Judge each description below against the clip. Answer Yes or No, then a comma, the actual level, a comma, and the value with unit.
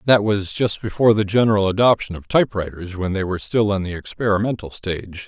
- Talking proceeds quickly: No, average, 195 wpm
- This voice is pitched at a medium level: No, low, 100 Hz